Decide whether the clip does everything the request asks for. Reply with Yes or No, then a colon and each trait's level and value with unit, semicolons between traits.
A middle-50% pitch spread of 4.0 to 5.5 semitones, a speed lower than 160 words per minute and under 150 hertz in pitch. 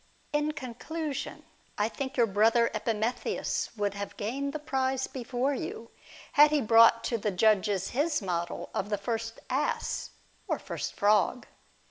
No: average, 4.4 semitones; average, 145 wpm; high, 230 Hz